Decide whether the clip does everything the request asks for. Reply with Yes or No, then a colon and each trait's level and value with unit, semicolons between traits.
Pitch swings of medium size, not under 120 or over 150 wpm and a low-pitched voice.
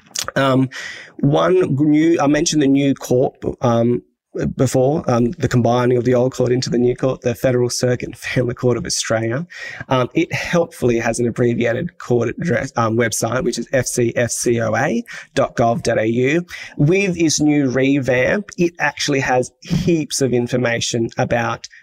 Yes: average, 3.3 semitones; average, 145 wpm; low, 125 Hz